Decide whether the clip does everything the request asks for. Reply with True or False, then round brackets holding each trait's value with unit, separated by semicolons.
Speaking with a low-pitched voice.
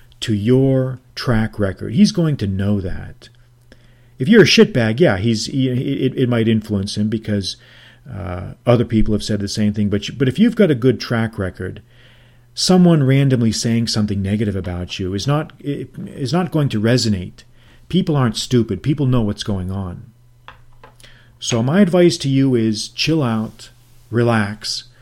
True (120 Hz)